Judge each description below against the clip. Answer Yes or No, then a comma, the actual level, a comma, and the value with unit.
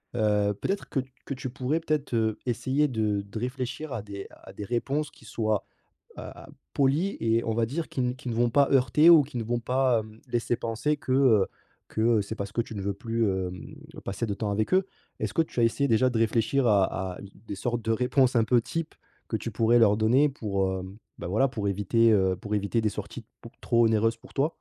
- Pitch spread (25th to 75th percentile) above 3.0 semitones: Yes, average, 3.7 semitones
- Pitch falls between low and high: No, low, 115 Hz